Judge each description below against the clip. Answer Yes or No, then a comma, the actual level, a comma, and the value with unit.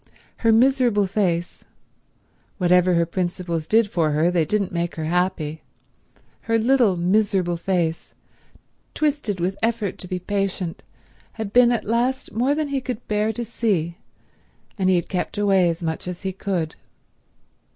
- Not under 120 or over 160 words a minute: Yes, average, 145 wpm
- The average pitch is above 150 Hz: Yes, high, 190 Hz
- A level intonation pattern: No, average, 4.5 semitones